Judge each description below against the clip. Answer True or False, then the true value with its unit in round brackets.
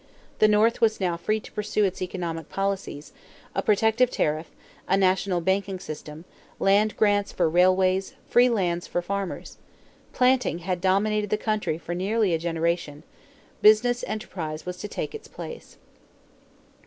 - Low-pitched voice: False (190 Hz)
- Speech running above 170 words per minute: False (145 wpm)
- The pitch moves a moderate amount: True (3.5 semitones)